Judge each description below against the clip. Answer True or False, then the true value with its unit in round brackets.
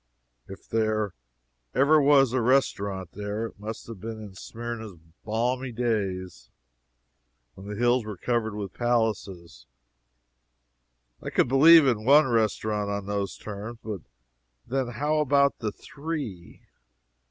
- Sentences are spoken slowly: True (130 wpm)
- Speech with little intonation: False (3.8 semitones)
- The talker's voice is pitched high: False (110 Hz)